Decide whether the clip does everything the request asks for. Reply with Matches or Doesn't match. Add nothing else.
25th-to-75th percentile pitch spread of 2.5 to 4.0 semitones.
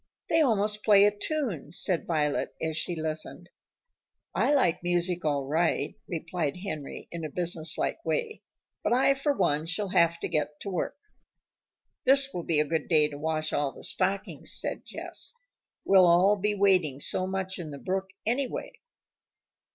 Doesn't match